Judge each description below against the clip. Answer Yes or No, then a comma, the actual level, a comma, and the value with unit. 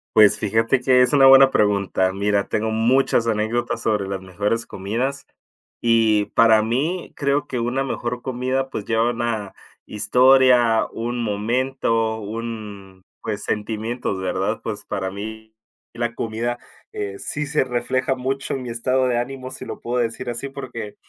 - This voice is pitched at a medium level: No, low, 115 Hz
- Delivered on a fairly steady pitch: No, average, 3.2 semitones